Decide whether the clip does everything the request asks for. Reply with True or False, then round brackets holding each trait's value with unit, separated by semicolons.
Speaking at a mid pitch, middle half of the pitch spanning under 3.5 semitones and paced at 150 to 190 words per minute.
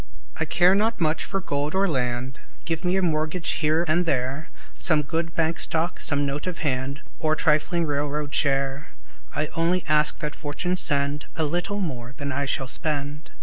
True (155 Hz; 3.0 semitones; 180 wpm)